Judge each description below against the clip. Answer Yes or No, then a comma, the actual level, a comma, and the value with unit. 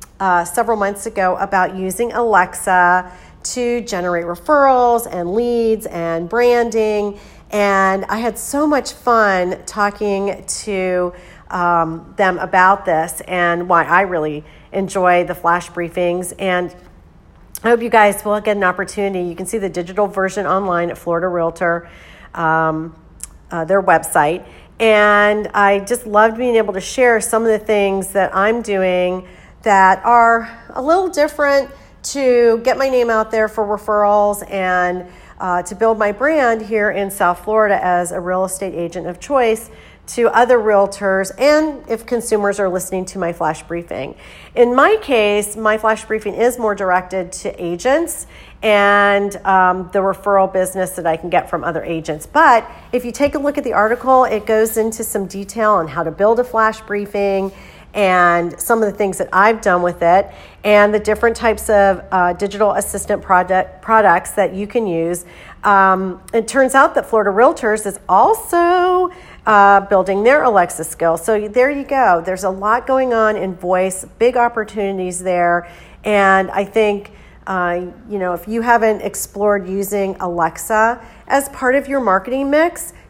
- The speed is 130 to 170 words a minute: Yes, average, 165 wpm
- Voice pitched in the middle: No, high, 200 Hz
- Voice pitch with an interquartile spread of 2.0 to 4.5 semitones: Yes, average, 3.7 semitones